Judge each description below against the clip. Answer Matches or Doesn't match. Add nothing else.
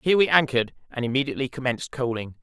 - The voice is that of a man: Matches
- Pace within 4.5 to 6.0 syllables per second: Doesn't match